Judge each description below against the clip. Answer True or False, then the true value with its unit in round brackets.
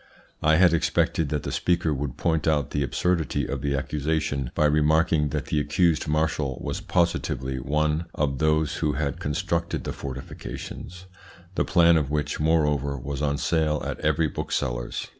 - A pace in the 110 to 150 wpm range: False (160 wpm)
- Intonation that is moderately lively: False (2.2 semitones)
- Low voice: True (75 Hz)